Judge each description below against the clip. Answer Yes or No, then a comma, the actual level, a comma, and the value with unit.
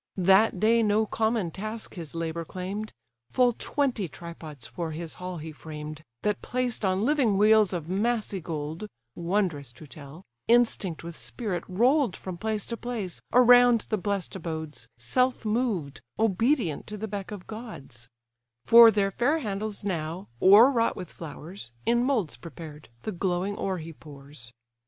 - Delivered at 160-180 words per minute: No, average, 150 wpm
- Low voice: No, high, 195 Hz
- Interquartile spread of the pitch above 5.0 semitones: Yes, wide, 5.4 semitones